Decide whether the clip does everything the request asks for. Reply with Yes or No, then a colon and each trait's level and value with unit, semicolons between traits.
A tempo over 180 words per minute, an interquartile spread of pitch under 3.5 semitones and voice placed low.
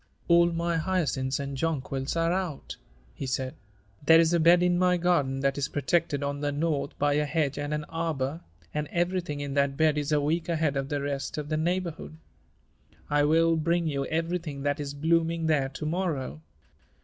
No: average, 190 wpm; average, 2.9 semitones; medium, 155 Hz